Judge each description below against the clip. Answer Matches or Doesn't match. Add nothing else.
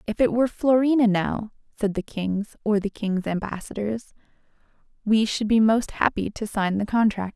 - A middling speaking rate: Matches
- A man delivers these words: Doesn't match